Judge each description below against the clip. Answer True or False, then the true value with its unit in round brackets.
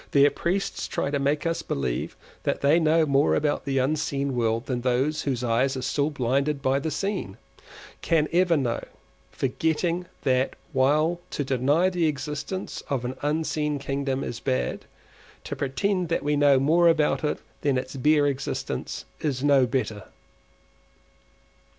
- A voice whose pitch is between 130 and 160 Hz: True (140 Hz)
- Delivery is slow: False (150 wpm)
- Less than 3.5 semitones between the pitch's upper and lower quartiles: True (3.0 semitones)